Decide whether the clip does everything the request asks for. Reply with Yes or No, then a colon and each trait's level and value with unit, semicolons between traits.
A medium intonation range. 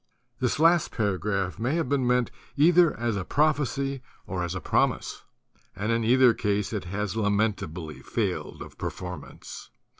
No: wide, 5.9 semitones